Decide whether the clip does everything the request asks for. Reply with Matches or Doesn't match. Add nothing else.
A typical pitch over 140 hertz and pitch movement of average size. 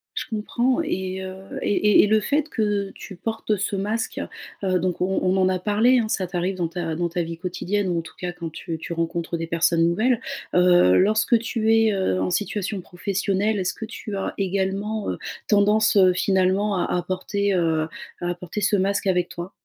Matches